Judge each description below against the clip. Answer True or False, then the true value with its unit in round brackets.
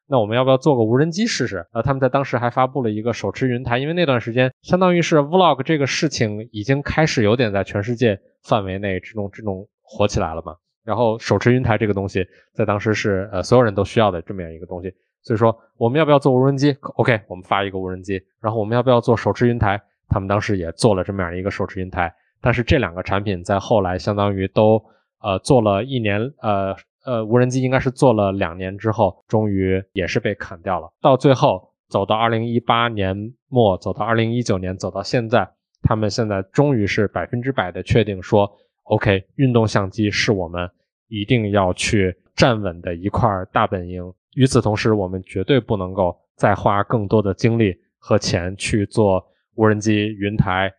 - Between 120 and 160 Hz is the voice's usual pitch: False (105 Hz)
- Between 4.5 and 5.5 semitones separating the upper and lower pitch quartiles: False (3.9 semitones)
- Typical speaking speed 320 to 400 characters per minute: True (325 characters per minute)